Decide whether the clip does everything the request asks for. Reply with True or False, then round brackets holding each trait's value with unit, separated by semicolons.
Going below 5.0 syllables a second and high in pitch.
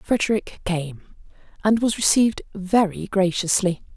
True (4.3 syllables/s; 195 Hz)